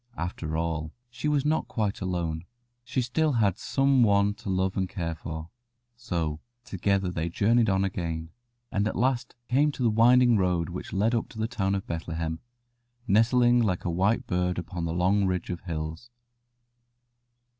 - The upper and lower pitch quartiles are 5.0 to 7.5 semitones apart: Yes, wide, 5.5 semitones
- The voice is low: Yes, very low, 95 Hz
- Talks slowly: No, average, 170 wpm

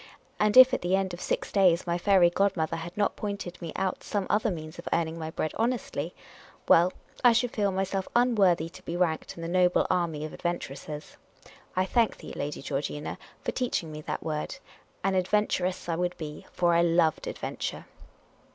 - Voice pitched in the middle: Yes, medium, 180 Hz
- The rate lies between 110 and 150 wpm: No, average, 190 wpm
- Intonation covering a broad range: No, average, 3.1 semitones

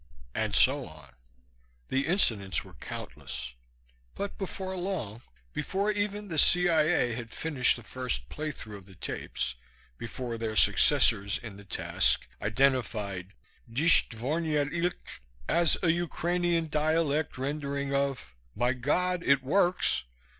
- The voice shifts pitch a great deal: Yes, wide, 7.1 semitones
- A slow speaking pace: Yes, slow, 125 wpm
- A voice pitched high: No, medium, 140 Hz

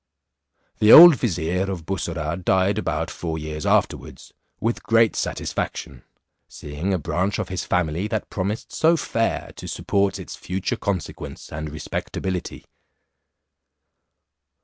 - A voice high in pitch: No, very low, 95 Hz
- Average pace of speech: No, slow, 125 wpm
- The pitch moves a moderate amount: Yes, average, 4.4 semitones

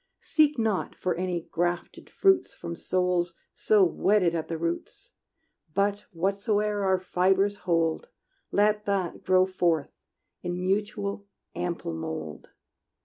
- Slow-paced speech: Yes, slow, 120 wpm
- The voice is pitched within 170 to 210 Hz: Yes, medium, 185 Hz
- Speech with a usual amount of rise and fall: Yes, average, 3.0 semitones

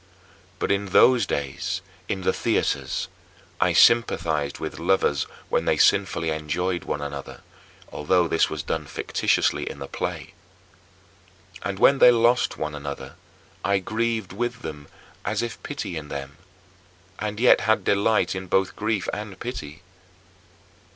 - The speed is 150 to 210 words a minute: No, slow, 135 wpm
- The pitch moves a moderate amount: No, wide, 6.3 semitones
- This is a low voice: Yes, very low, 95 Hz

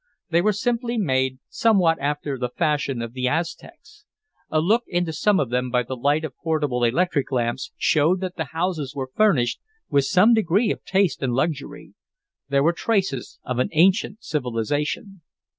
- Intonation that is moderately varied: No, wide, 6.1 semitones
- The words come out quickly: No, average, 170 wpm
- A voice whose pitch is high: No, medium, 155 Hz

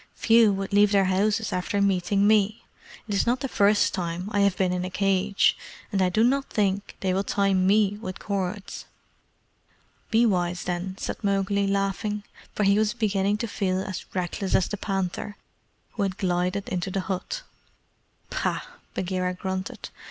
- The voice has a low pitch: No, high, 195 Hz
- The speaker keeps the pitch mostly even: Yes, narrow, 1.8 semitones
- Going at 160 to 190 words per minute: Yes, average, 170 wpm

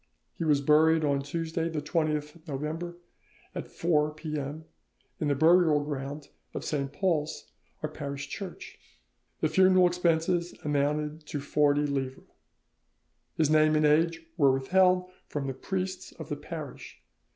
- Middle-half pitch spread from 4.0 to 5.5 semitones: No, narrow, 2.5 semitones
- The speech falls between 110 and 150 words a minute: Yes, average, 140 wpm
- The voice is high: No, medium, 155 Hz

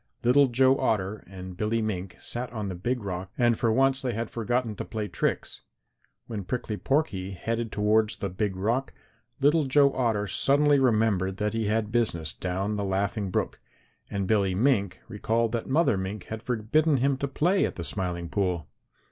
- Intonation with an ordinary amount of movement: Yes, average, 4.3 semitones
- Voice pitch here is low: Yes, low, 110 Hz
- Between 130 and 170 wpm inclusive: No, average, 180 wpm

